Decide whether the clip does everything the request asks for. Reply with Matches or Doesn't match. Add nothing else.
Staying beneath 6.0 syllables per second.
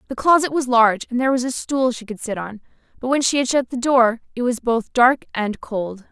Matches